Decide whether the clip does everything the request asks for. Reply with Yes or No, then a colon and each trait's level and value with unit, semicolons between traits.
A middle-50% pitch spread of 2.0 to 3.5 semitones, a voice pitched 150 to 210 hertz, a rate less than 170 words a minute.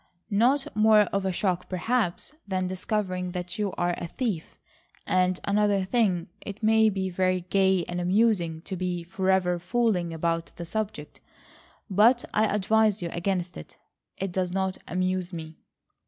Yes: average, 2.9 semitones; medium, 185 Hz; average, 155 wpm